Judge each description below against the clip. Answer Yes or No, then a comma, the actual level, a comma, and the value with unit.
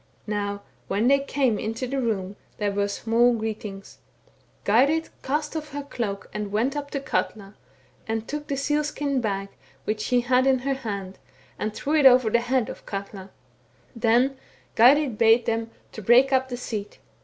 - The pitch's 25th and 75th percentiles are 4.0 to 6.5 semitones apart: Yes, average, 4.3 semitones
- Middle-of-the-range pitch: No, high, 235 Hz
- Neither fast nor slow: Yes, average, 180 wpm